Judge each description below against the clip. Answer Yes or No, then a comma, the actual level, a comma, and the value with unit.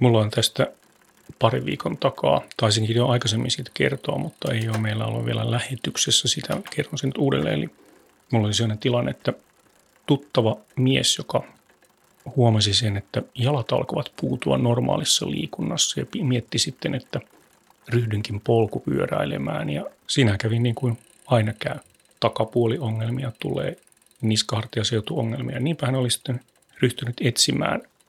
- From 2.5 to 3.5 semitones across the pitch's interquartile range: Yes, average, 2.8 semitones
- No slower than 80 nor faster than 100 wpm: No, average, 135 wpm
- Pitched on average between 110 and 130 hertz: Yes, low, 120 Hz